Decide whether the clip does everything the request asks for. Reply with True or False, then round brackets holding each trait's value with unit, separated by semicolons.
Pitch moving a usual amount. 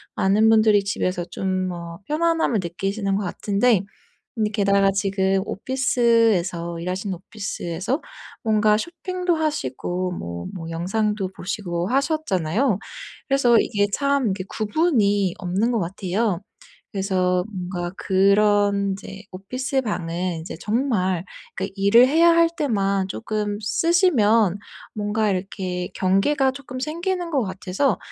True (4.4 semitones)